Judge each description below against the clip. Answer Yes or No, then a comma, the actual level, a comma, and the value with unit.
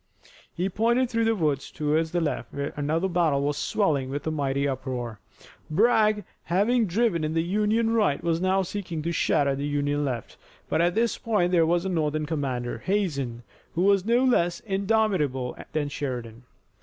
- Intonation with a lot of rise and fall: Yes, wide, 5.9 semitones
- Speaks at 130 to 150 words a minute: No, average, 175 wpm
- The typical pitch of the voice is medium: Yes, medium, 165 Hz